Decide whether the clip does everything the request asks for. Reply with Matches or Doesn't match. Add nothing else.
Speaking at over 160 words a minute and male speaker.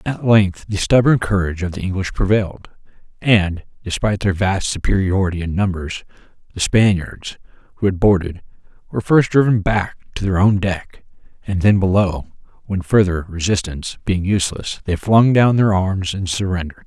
Doesn't match